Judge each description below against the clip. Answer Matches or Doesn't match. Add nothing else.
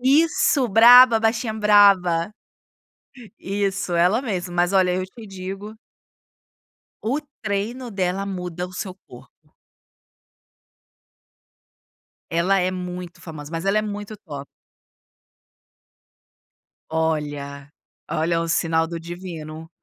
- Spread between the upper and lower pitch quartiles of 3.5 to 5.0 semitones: Matches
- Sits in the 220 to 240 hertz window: Doesn't match